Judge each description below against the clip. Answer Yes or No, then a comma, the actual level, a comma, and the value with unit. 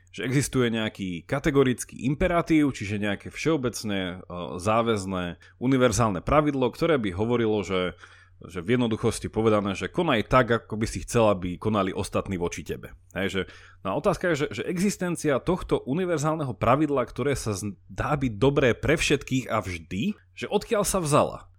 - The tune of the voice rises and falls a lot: Yes, wide, 7.1 semitones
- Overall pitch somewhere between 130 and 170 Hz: No, low, 110 Hz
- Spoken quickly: No, average, 145 wpm